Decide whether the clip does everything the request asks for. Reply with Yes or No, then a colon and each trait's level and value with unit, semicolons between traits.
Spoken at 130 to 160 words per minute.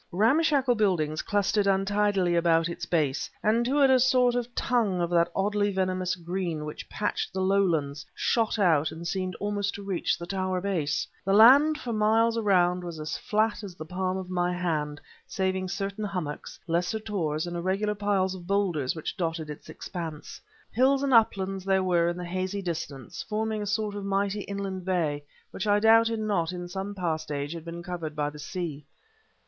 No: average, 185 wpm